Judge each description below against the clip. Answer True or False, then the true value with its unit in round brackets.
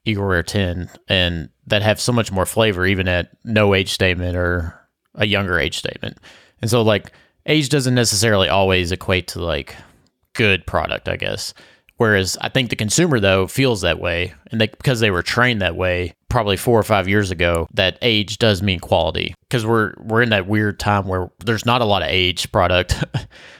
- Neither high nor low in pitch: False (100 Hz)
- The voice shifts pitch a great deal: False (3.8 semitones)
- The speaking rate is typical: True (195 wpm)